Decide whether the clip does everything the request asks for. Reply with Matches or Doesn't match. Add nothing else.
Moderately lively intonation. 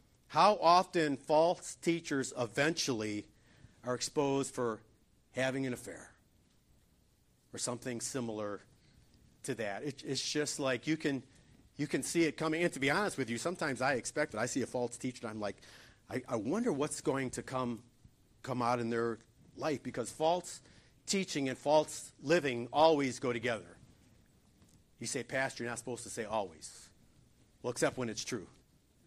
Matches